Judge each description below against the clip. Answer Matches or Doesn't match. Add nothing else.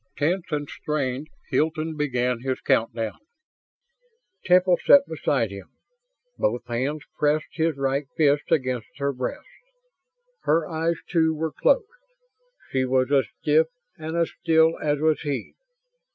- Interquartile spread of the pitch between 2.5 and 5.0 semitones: Matches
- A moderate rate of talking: Doesn't match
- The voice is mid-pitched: Matches